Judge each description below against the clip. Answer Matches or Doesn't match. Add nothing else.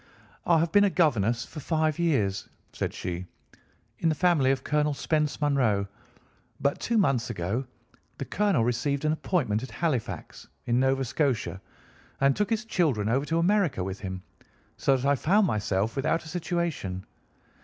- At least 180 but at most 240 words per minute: Doesn't match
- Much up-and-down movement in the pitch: Matches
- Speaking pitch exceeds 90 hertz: Matches